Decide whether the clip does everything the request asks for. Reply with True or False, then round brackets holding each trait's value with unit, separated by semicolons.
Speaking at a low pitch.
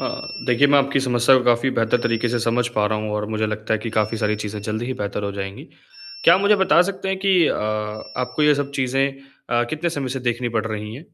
True (120 Hz)